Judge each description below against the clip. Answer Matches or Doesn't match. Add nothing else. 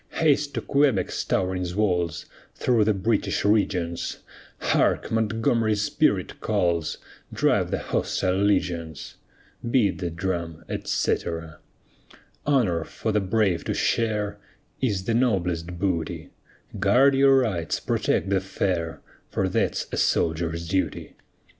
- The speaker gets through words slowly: Matches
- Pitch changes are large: Doesn't match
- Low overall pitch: Matches